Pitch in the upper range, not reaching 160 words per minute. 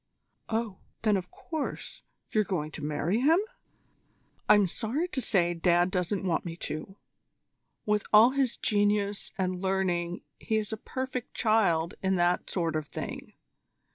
Yes: high, 195 Hz; average, 145 wpm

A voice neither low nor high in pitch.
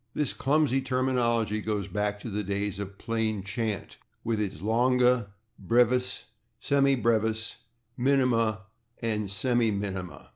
No: low, 115 Hz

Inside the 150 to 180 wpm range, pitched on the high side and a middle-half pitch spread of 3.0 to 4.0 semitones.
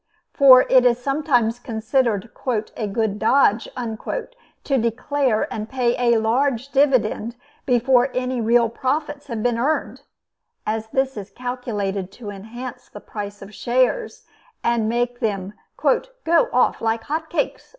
No: average, 140 wpm; high, 240 Hz; average, 3.3 semitones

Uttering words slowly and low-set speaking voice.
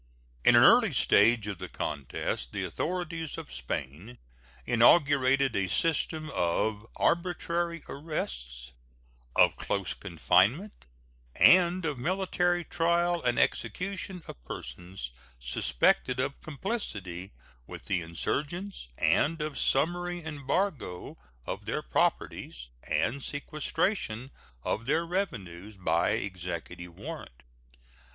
Yes: slow, 105 wpm; low, 130 Hz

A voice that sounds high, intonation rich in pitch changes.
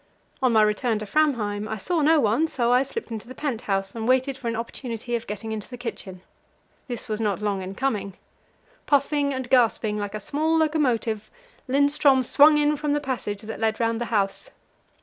No: high, 235 Hz; average, 4.8 semitones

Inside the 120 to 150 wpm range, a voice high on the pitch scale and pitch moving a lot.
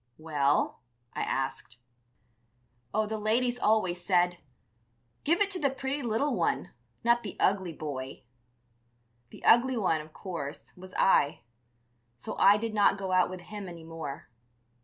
Yes: average, 145 wpm; high, 195 Hz; wide, 5.8 semitones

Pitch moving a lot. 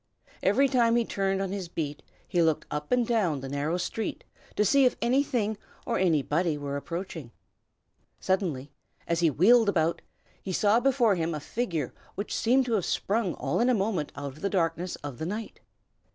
Yes: wide, 6.2 semitones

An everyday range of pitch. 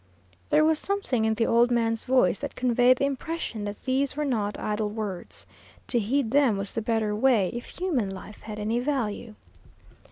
Yes: average, 3.9 semitones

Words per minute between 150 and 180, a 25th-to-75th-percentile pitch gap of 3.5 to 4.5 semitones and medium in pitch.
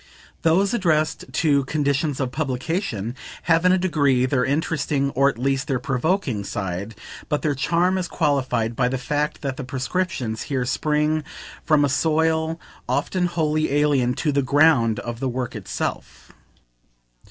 Yes: average, 155 wpm; average, 4.0 semitones; medium, 145 Hz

